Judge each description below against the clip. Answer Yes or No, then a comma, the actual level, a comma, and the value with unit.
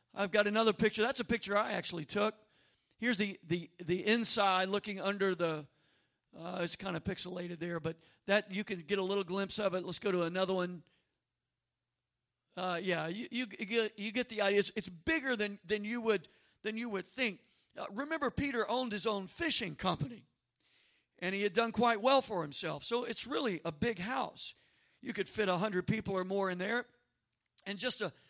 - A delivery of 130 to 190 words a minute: No, average, 200 wpm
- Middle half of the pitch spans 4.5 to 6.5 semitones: No, average, 3.8 semitones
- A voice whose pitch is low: No, high, 200 Hz